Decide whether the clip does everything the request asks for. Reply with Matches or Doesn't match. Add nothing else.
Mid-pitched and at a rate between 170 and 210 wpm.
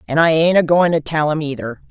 Doesn't match